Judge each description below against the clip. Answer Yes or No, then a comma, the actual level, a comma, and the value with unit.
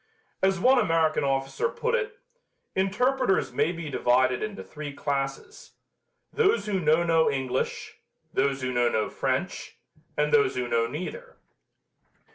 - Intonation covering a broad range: Yes, wide, 6.9 semitones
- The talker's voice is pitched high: No, medium, 155 Hz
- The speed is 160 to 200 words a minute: No, slow, 135 wpm